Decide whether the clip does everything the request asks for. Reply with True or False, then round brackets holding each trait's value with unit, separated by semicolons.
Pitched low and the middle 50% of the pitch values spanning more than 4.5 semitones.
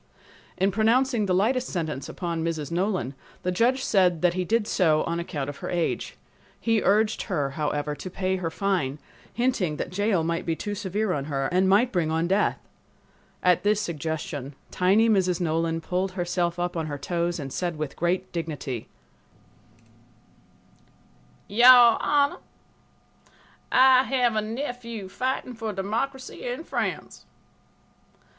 False (185 Hz; 5.0 semitones)